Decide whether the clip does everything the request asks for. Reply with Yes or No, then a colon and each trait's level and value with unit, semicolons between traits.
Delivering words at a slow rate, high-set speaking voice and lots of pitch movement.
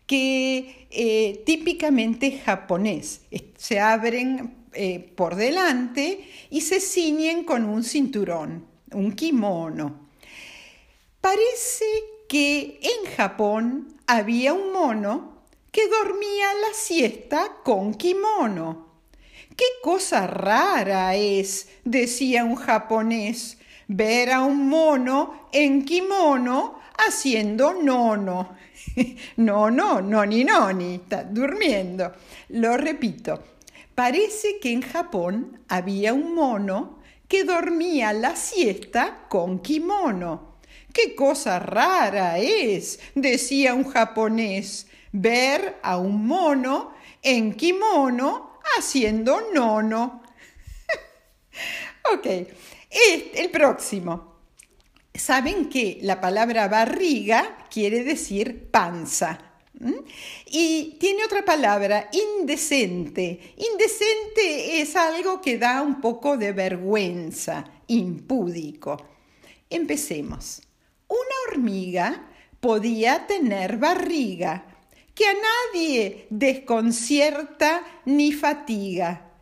Yes: slow, 95 wpm; very high, 260 Hz; wide, 7.1 semitones